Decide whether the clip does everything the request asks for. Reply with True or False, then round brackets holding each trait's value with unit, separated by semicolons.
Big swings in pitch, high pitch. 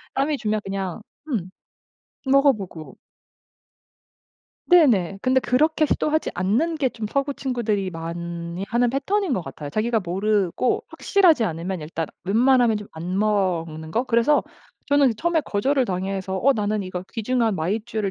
True (6.2 semitones; 215 Hz)